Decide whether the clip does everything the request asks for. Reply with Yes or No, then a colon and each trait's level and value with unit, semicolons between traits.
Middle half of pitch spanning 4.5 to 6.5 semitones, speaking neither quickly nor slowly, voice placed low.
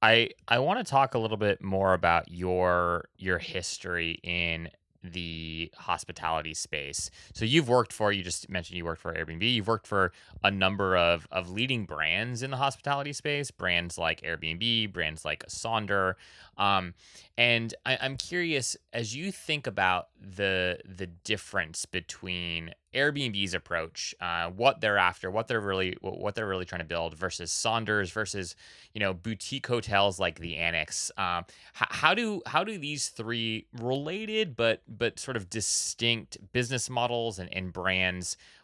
Yes: average, 5.1 semitones; average, 160 wpm; low, 100 Hz